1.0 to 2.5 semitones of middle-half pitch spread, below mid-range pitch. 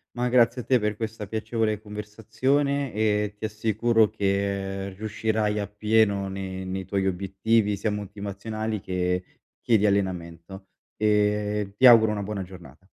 Yes: narrow, 2.1 semitones; low, 105 Hz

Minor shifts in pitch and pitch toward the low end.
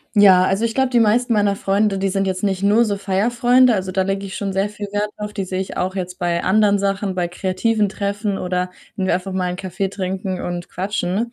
No: narrow, 2.0 semitones; high, 195 Hz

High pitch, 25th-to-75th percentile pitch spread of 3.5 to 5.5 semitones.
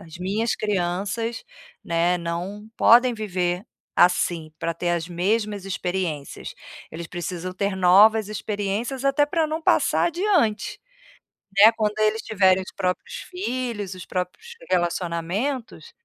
Yes: high, 200 Hz; average, 4.2 semitones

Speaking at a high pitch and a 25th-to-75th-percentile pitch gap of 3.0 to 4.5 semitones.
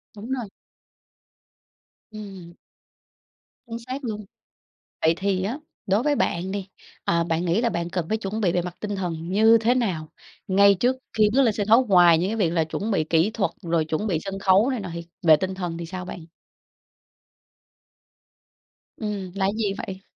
Yes: high, 195 Hz; average, 4.0 semitones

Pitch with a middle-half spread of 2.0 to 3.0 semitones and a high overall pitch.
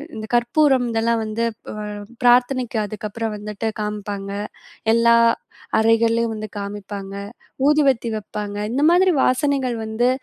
Yes: average, 2.7 semitones; high, 225 Hz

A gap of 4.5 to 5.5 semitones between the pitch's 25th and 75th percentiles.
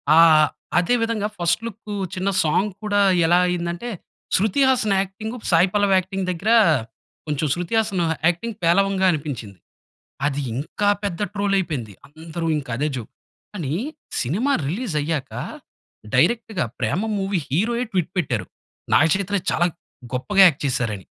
Yes: average, 5.1 semitones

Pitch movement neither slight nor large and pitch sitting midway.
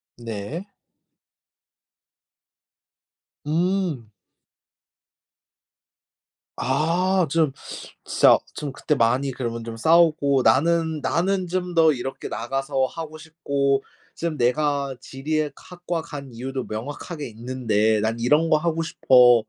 Yes: average, 4.7 semitones; medium, 145 Hz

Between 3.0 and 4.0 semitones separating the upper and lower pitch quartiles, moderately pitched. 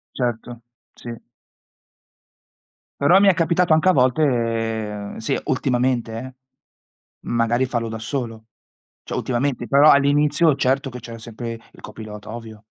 No: average, 3.7 semitones; low, 120 Hz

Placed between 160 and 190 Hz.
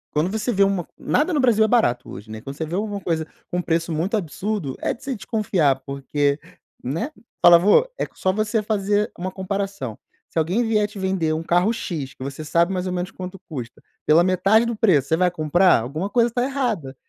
Yes: medium, 185 Hz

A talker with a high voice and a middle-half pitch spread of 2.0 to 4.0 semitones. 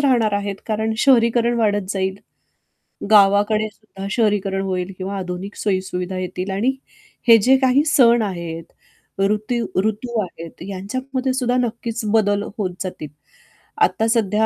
Yes: high, 210 Hz; average, 3.4 semitones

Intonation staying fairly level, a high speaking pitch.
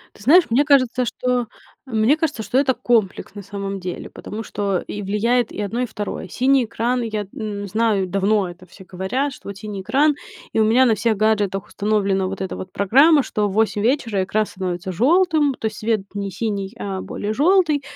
No: average, 4.1 semitones; high, 215 Hz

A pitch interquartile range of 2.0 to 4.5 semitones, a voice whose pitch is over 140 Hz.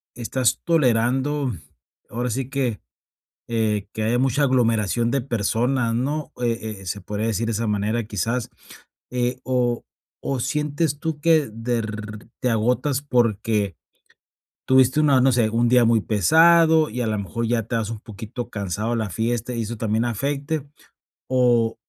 No: average, 2.9 semitones; low, 120 Hz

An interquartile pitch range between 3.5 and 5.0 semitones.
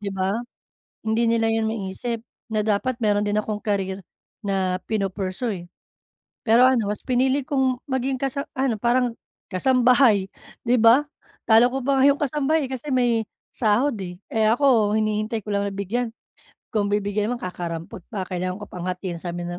Yes: average, 4.0 semitones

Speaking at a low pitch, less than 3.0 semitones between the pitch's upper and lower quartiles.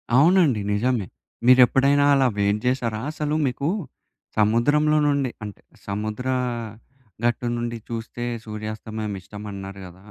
No: low, 120 Hz; average, 4.2 semitones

